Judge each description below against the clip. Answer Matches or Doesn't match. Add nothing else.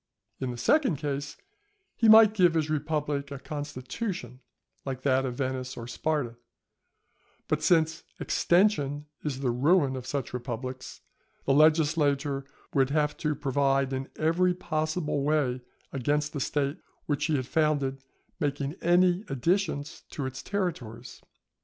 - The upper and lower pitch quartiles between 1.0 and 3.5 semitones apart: Matches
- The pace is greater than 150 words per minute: Doesn't match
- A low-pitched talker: Doesn't match